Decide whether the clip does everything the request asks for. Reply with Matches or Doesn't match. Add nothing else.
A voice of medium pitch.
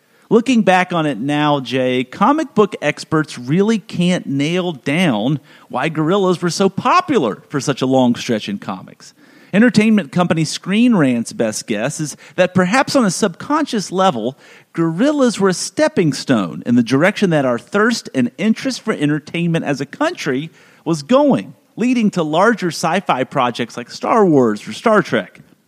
Matches